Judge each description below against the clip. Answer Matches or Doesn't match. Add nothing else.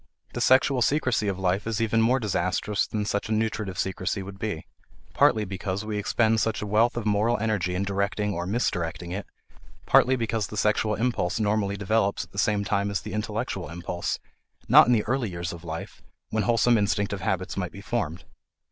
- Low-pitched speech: Matches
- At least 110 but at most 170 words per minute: Doesn't match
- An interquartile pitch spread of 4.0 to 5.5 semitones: Doesn't match